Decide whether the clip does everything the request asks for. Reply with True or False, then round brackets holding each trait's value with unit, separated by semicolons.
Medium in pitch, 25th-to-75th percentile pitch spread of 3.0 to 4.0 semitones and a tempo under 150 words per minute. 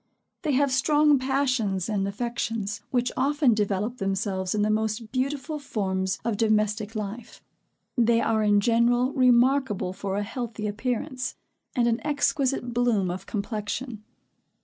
False (230 Hz; 3.7 semitones; 135 wpm)